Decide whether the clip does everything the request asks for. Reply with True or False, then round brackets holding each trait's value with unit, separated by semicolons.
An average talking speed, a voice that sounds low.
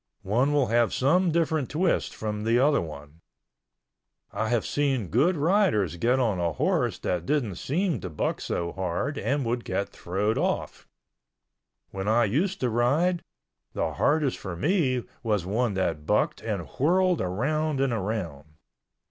True (155 wpm; 120 Hz)